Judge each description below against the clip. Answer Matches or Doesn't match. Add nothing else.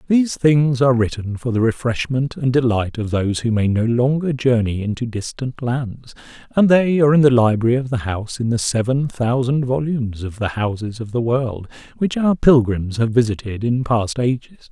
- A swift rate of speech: Doesn't match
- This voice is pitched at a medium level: Doesn't match